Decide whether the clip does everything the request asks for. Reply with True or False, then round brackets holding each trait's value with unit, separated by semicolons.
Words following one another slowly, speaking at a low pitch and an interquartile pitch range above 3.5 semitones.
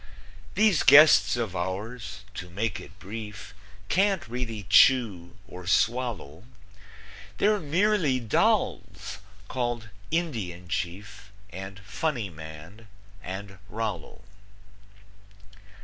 True (90 wpm; 105 Hz; 5.1 semitones)